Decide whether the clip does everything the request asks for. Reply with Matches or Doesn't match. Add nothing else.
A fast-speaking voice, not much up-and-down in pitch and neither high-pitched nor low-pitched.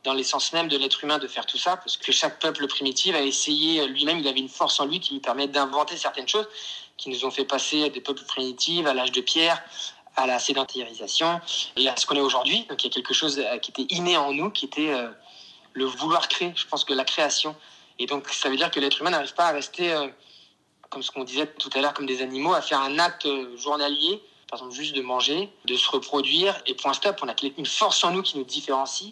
Doesn't match